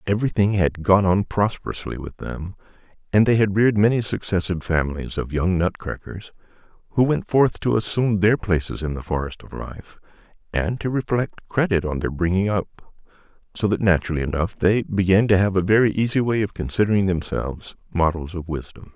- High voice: No, very low, 95 Hz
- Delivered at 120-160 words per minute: No, average, 170 wpm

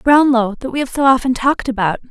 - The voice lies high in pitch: Yes, very high, 250 Hz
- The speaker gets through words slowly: No, fast, 230 wpm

